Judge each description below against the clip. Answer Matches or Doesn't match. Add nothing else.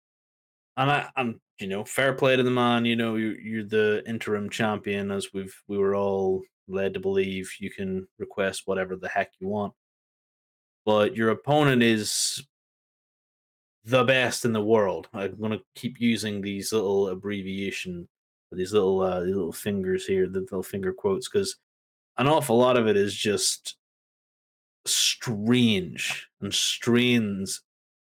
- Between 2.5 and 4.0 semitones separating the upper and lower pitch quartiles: Doesn't match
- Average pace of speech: Matches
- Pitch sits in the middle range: Doesn't match